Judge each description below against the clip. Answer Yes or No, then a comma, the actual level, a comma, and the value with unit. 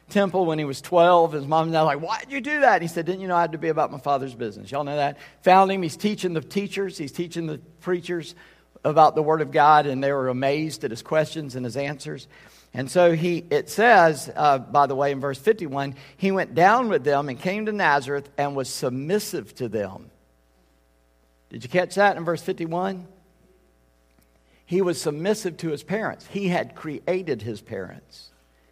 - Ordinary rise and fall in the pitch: Yes, average, 4.7 semitones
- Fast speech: Yes, fast, 210 wpm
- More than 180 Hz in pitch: No, medium, 155 Hz